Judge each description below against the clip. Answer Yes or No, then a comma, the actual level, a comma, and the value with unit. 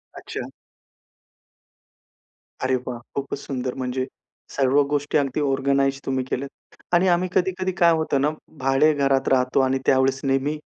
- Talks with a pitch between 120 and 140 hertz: Yes, low, 135 Hz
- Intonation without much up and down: Yes, narrow, 1.9 semitones